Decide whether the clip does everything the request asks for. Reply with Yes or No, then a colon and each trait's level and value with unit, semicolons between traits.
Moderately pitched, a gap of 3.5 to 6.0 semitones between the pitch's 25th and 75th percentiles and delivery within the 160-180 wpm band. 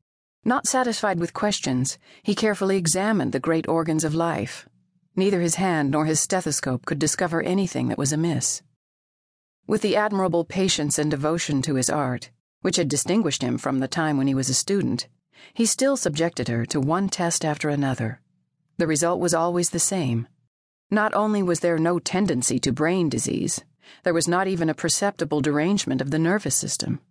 Yes: medium, 165 Hz; average, 4.4 semitones; average, 175 wpm